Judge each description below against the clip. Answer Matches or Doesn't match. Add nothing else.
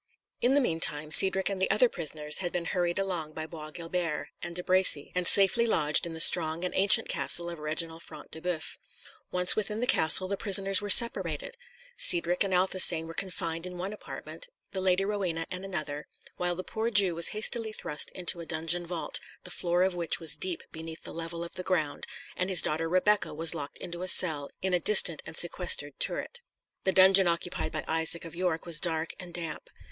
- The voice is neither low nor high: Matches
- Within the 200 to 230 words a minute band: Matches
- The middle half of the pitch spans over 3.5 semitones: Doesn't match